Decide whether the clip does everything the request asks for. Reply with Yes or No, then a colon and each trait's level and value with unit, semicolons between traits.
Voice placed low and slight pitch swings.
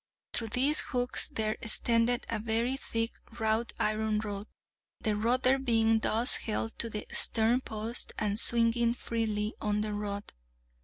No: high, 225 Hz; narrow, 1.7 semitones